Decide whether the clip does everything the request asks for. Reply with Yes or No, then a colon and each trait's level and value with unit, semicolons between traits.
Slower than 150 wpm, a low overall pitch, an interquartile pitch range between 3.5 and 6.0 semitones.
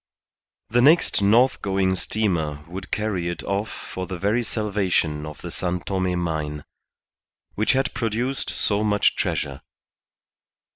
Yes: slow, 135 wpm; very low, 95 Hz; average, 3.9 semitones